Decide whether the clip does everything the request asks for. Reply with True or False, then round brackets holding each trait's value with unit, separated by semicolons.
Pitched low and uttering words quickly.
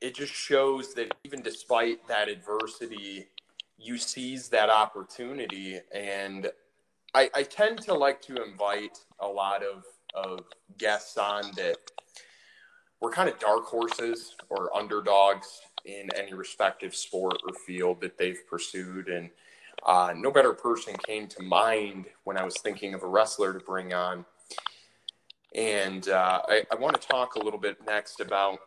False (100 Hz; 155 wpm)